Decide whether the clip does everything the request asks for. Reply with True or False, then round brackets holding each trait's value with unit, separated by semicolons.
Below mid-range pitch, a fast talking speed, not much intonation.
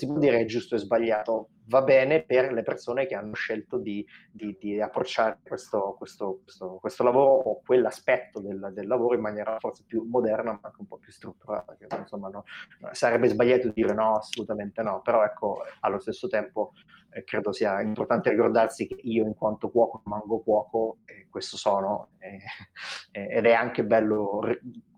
True (110 Hz; 180 wpm; 2.2 semitones)